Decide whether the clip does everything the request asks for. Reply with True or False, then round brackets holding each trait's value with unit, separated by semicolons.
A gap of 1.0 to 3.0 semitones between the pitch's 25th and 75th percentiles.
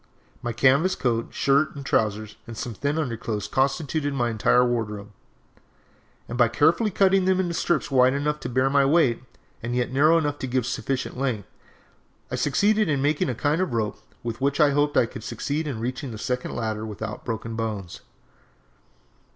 False (4.2 semitones)